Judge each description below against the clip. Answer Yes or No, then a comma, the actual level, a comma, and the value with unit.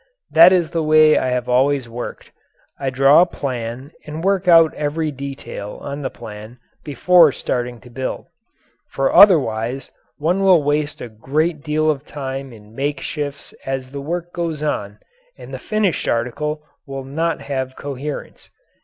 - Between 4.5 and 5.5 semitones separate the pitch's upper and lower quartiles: No, average, 3.3 semitones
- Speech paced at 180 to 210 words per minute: No, average, 155 wpm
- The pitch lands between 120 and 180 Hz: Yes, medium, 140 Hz